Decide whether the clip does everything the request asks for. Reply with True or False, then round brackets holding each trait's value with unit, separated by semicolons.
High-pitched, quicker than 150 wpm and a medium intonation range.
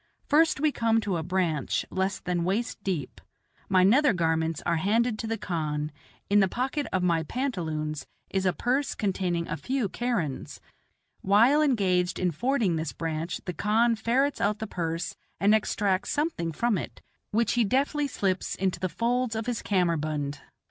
False (195 Hz; 170 wpm; 5.8 semitones)